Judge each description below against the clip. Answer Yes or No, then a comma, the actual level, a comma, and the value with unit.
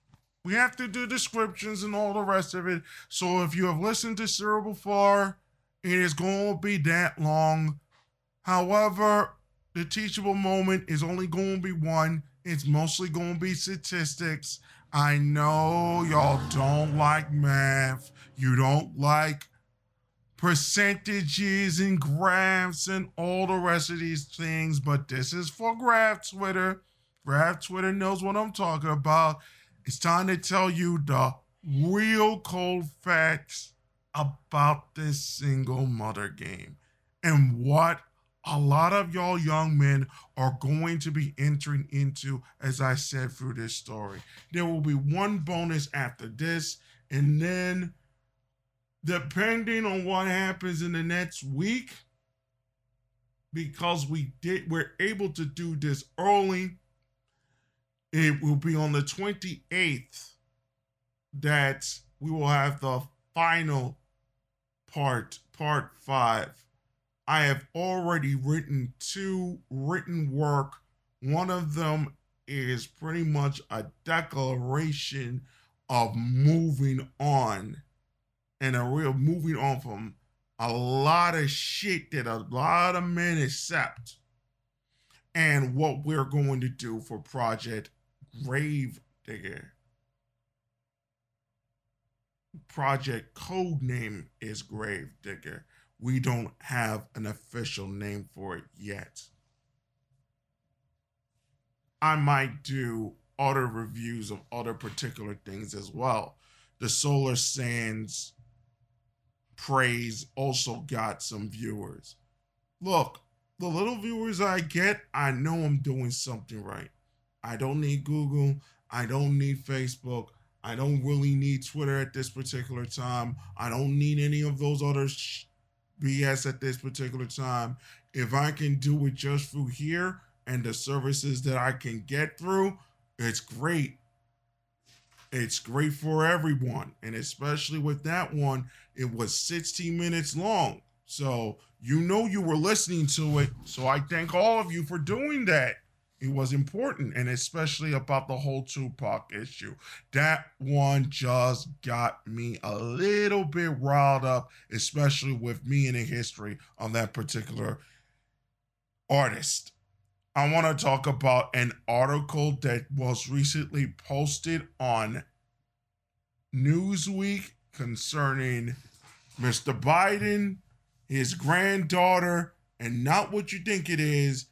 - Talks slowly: Yes, slow, 130 wpm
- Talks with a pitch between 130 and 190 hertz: Yes, medium, 140 Hz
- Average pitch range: Yes, average, 4.6 semitones